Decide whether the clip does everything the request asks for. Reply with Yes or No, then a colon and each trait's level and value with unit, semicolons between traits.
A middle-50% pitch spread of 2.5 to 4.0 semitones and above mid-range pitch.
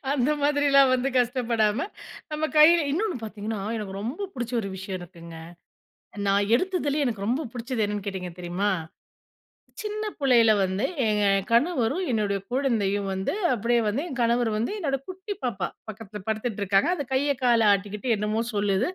No: average, 5.3 semitones; high, 230 Hz